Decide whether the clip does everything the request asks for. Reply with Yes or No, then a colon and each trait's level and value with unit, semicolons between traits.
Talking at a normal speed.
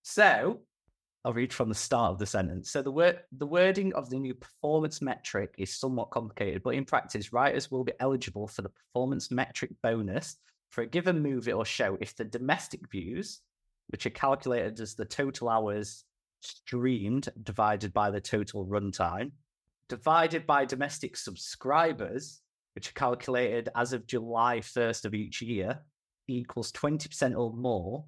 Yes: average, 160 wpm